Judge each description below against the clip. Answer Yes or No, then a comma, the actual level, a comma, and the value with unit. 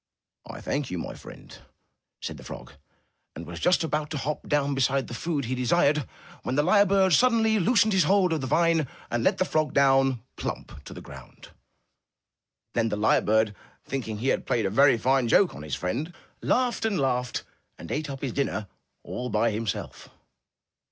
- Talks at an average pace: Yes, average, 190 wpm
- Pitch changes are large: Yes, wide, 6.2 semitones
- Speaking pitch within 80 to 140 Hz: Yes, low, 135 Hz